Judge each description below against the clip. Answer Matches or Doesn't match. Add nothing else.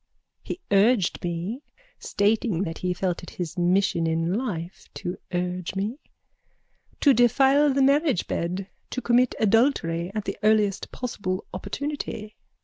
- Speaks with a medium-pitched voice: Doesn't match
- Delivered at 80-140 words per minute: Matches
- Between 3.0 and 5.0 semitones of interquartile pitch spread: Doesn't match